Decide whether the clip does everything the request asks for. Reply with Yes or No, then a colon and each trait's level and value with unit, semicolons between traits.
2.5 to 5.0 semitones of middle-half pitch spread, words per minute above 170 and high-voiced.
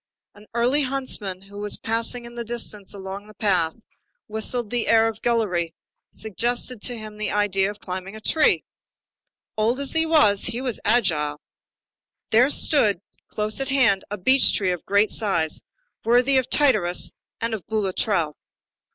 No: average, 3.5 semitones; average, 160 wpm; high, 215 Hz